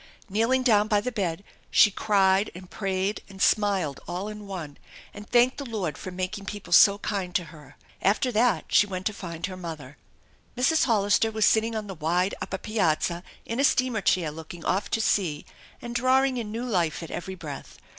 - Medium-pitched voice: No, high, 200 Hz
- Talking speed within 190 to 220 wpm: Yes, average, 195 wpm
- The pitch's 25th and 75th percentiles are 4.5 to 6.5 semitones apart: No, average, 3.8 semitones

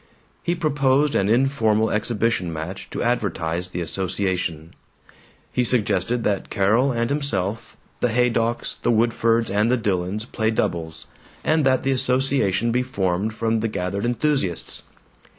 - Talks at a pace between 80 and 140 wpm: Yes, slow, 135 wpm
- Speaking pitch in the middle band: No, low, 110 Hz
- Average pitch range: Yes, average, 4.6 semitones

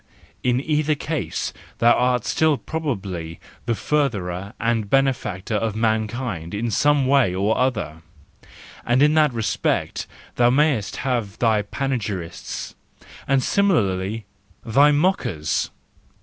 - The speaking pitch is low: Yes, low, 120 Hz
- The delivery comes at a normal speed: No, slow, 110 wpm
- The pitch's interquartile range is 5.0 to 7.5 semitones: Yes, wide, 5.4 semitones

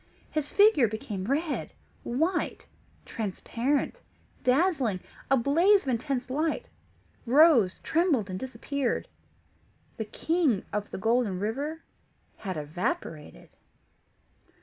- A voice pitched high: Yes, very high, 260 Hz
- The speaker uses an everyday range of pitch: No, wide, 6.6 semitones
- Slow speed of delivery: Yes, slow, 100 wpm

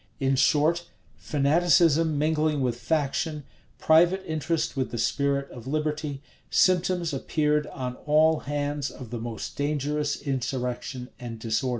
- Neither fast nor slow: No, slow, 125 wpm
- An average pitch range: Yes, average, 3.1 semitones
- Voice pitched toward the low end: No, medium, 145 Hz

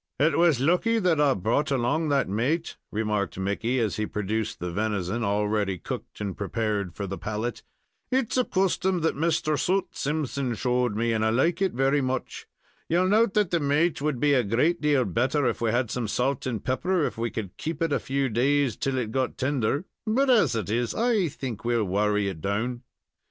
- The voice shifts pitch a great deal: Yes, wide, 6.3 semitones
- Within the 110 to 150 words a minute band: No, fast, 205 wpm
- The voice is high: No, low, 130 Hz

